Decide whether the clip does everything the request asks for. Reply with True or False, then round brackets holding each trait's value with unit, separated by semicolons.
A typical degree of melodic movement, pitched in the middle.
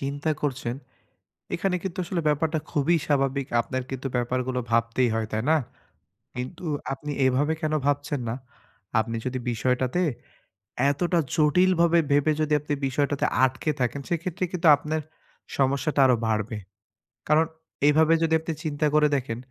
True (3.6 semitones; 145 Hz)